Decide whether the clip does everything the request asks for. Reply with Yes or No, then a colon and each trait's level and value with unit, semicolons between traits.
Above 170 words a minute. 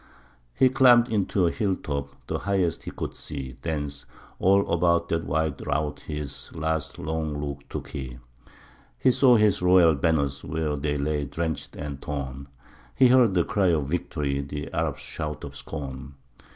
No: average, 165 wpm